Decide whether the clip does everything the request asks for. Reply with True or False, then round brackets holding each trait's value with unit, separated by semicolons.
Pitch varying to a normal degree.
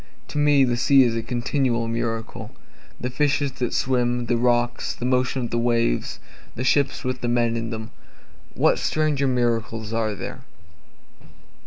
False (1.9 semitones)